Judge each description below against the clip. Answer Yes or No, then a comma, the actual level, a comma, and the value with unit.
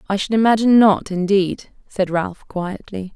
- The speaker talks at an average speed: Yes, average, 150 wpm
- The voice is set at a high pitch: Yes, high, 195 Hz